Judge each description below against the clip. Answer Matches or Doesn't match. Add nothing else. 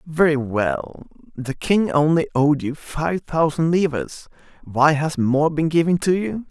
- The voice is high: Doesn't match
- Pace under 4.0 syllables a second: Matches